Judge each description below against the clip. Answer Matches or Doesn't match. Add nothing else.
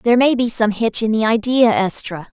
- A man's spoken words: Doesn't match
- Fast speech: Matches